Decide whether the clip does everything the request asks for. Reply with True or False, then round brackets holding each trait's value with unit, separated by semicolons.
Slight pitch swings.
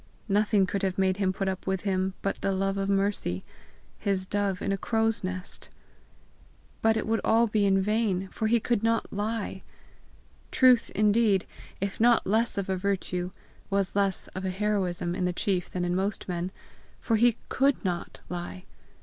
True (2.3 semitones)